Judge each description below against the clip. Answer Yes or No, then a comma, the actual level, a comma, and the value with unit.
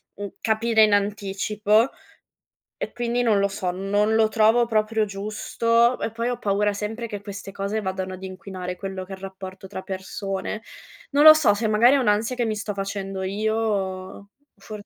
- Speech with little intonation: Yes, narrow, 2.2 semitones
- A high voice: Yes, high, 205 Hz